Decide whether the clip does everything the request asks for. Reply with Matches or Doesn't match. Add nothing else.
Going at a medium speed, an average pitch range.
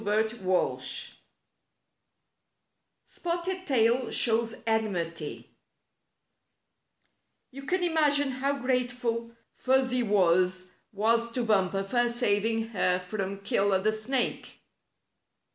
Doesn't match